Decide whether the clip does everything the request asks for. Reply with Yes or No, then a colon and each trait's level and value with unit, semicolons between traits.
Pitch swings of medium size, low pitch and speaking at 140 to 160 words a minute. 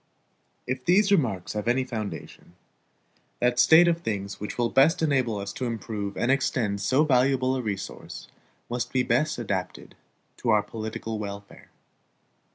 Yes: average, 4.1 semitones; low, 120 Hz; average, 150 wpm